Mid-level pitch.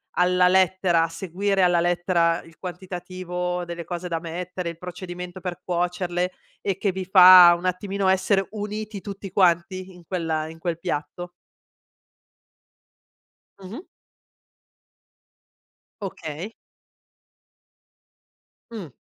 Yes: medium, 180 Hz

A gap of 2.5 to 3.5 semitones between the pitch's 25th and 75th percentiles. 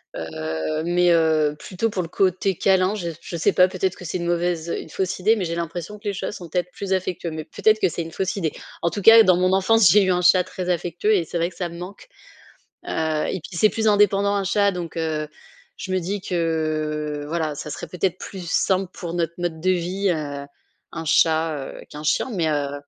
Yes: average, 2.9 semitones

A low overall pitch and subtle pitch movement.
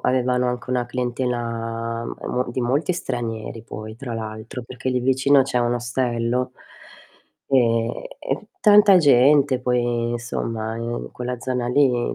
Yes: low, 125 Hz; narrow, 1.7 semitones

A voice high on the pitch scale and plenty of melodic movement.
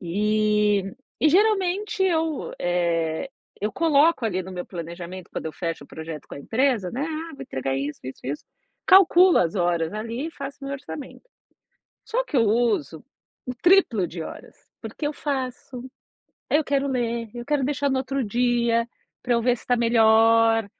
Yes: high, 235 Hz; wide, 7.3 semitones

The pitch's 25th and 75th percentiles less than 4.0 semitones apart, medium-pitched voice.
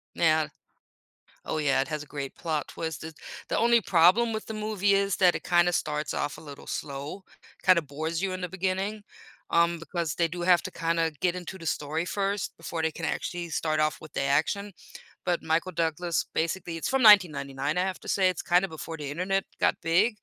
Yes: average, 3.2 semitones; medium, 170 Hz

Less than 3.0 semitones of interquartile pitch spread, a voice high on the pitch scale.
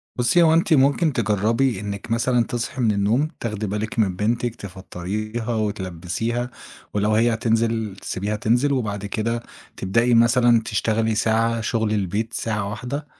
No: narrow, 2.4 semitones; low, 115 Hz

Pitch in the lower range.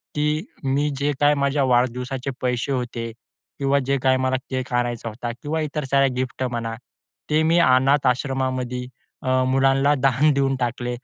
Yes: low, 130 Hz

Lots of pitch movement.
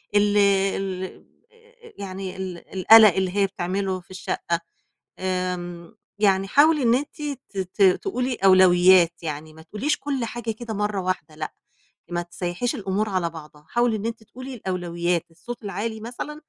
No: average, 3.8 semitones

